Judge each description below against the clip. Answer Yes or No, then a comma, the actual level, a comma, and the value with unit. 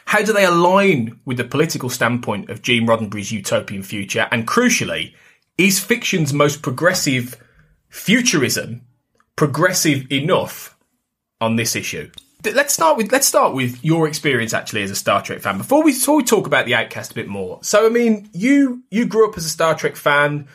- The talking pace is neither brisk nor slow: Yes, average, 175 wpm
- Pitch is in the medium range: Yes, medium, 150 Hz